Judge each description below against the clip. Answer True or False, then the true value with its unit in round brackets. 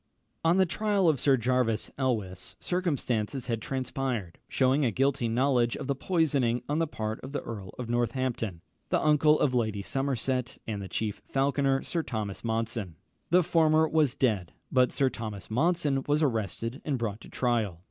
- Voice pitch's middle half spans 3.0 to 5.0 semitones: True (4.1 semitones)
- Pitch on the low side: True (130 Hz)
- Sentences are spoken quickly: False (170 wpm)